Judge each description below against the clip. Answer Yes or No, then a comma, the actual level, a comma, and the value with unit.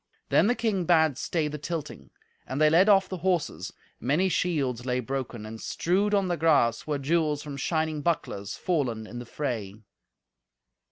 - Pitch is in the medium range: Yes, medium, 155 Hz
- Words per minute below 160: No, average, 170 wpm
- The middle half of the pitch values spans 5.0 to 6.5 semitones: Yes, average, 5.3 semitones